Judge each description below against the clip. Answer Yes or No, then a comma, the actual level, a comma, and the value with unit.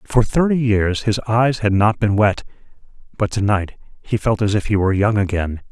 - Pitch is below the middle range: Yes, low, 105 Hz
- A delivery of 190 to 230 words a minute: Yes, average, 200 wpm